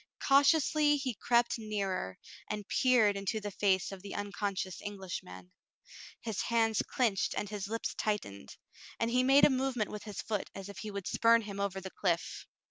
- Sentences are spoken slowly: No, average, 180 wpm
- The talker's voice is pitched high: Yes, high, 210 Hz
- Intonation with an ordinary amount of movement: Yes, average, 3.1 semitones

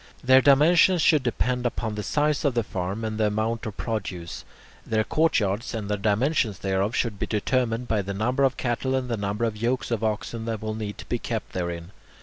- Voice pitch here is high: No, low, 115 Hz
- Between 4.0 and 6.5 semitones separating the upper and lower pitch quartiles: No, average, 3.3 semitones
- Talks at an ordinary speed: No, fast, 210 wpm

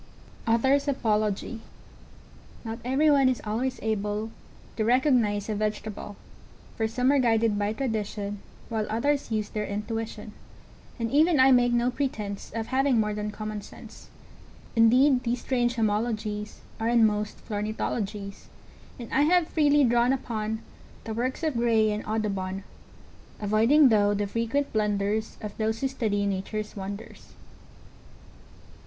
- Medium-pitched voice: No, high, 225 Hz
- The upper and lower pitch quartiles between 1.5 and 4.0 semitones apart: Yes, average, 3.0 semitones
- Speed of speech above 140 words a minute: No, slow, 135 wpm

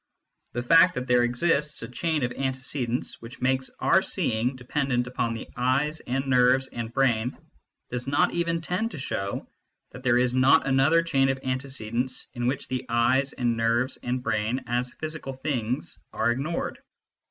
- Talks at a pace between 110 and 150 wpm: No, average, 165 wpm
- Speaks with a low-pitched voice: Yes, low, 130 Hz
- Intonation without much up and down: Yes, narrow, 2.2 semitones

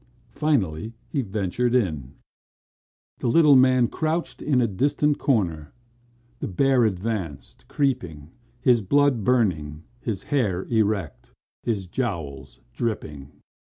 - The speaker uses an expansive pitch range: Yes, wide, 7.3 semitones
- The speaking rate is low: Yes, slow, 110 wpm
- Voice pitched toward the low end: Yes, low, 110 Hz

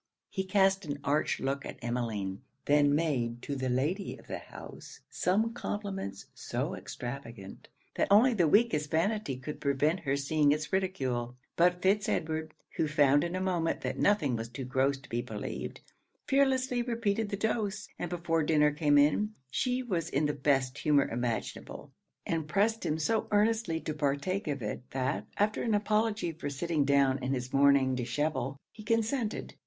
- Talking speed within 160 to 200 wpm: Yes, average, 170 wpm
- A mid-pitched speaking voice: Yes, medium, 155 Hz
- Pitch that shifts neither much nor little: No, wide, 6.6 semitones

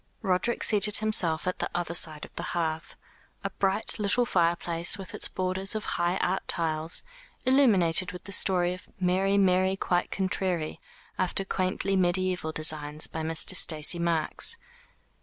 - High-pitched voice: No, medium, 180 Hz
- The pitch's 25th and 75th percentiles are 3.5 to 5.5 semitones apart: No, narrow, 2.5 semitones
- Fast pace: No, average, 155 wpm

